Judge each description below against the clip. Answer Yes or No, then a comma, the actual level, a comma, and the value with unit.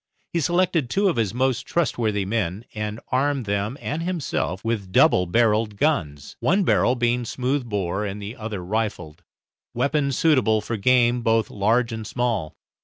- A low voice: Yes, low, 115 Hz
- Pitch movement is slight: No, average, 4.2 semitones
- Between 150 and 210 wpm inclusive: Yes, average, 160 wpm